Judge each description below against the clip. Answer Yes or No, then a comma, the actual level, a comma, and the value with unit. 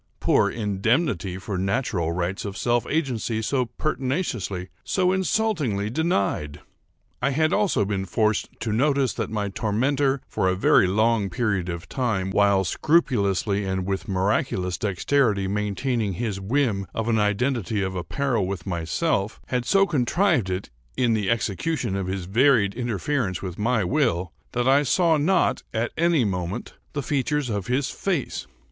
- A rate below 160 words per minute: Yes, average, 150 wpm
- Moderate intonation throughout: No, wide, 5.9 semitones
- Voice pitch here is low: Yes, low, 110 Hz